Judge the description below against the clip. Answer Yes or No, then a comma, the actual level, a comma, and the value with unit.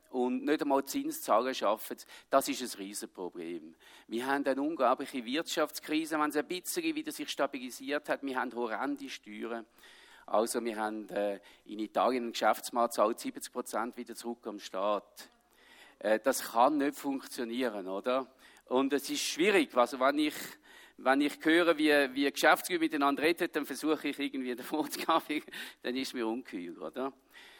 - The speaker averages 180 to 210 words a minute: No, average, 160 wpm